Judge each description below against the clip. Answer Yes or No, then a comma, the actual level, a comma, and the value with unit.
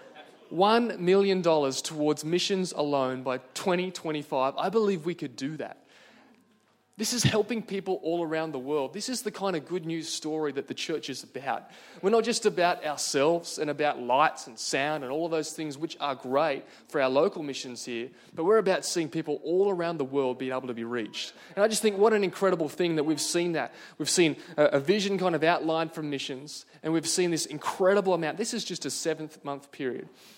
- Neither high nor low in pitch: Yes, medium, 160 Hz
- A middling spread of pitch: Yes, average, 4.1 semitones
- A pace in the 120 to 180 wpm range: No, fast, 205 wpm